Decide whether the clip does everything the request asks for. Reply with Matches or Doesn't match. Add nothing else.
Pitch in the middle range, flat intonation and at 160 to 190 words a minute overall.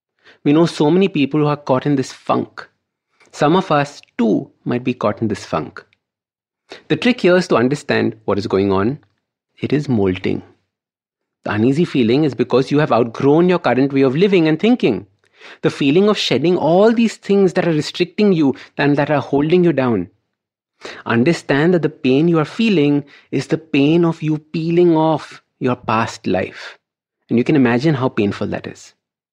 Doesn't match